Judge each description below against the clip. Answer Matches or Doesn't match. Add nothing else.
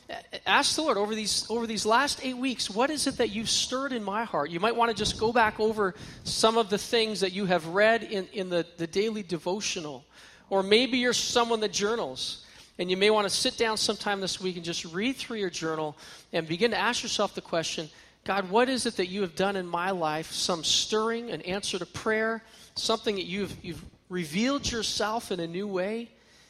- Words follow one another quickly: Matches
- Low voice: Doesn't match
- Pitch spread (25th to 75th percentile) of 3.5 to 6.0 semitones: Matches